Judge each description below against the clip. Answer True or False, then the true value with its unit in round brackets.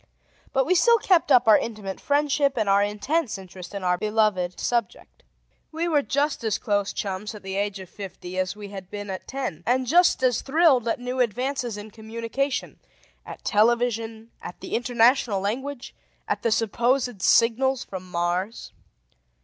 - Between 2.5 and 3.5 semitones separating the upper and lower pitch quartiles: False (4.6 semitones)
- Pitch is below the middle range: False (225 Hz)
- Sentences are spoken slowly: False (165 wpm)